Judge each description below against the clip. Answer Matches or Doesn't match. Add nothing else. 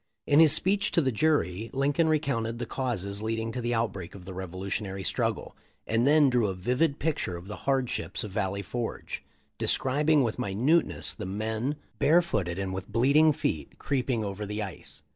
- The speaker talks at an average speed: Matches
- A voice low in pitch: Matches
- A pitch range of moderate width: Doesn't match